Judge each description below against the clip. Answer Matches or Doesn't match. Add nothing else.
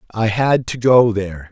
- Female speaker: Doesn't match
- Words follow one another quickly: Doesn't match